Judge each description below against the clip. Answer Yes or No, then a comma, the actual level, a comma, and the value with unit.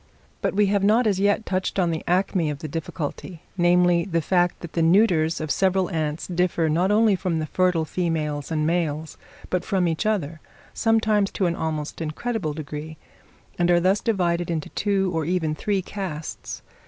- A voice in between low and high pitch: Yes, medium, 175 Hz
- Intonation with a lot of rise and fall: No, average, 3.3 semitones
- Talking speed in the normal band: Yes, average, 180 wpm